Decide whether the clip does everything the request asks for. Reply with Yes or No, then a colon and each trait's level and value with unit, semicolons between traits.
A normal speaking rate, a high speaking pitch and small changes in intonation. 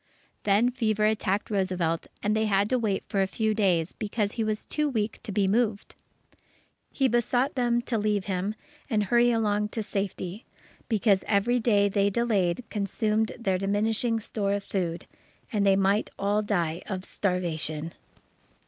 Yes: average, 160 wpm; high, 205 Hz; narrow, 2.3 semitones